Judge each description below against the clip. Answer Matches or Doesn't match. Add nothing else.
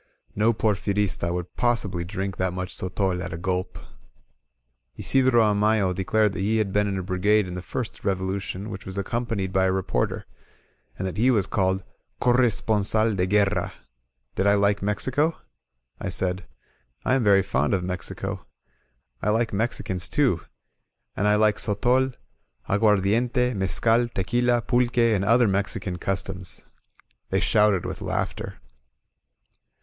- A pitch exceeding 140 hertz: Doesn't match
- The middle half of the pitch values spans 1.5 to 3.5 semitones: Matches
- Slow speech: Doesn't match